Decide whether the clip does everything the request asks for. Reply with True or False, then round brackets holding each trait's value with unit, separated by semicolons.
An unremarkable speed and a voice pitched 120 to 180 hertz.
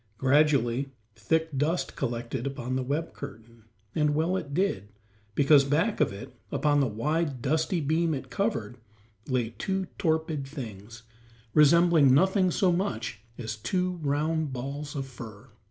True (145 wpm; 140 Hz)